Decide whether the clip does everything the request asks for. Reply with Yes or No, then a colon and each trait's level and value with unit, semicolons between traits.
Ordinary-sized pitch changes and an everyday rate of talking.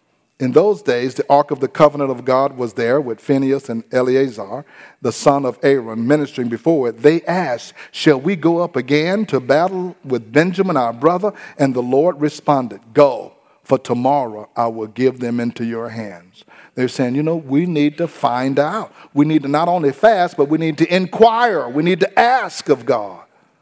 Yes: average, 4.6 semitones; average, 195 wpm